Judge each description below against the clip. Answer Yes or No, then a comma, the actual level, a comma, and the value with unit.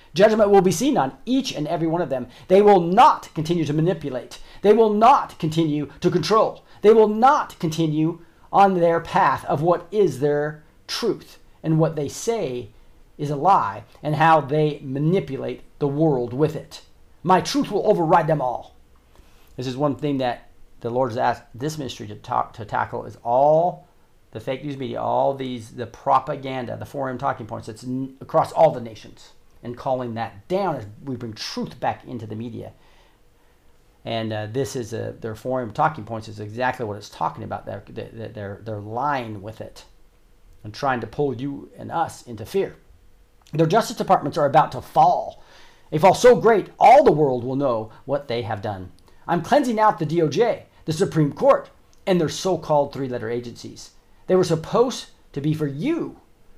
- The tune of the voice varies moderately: No, wide, 6.6 semitones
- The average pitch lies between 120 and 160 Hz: Yes, medium, 140 Hz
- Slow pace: No, average, 185 wpm